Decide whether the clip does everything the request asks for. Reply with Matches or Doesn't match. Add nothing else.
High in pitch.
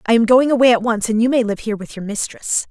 Matches